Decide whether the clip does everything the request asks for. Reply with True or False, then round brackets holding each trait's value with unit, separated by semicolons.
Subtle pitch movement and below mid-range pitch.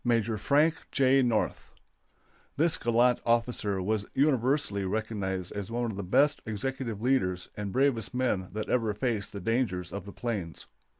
False (4.2 semitones; 115 Hz)